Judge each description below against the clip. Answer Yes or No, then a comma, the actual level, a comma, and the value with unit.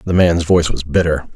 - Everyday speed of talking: No, fast, 220 wpm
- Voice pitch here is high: No, very low, 85 Hz